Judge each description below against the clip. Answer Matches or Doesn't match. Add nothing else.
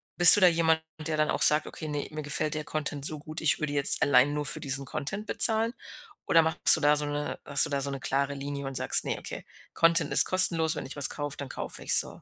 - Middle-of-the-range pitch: Matches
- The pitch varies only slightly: Matches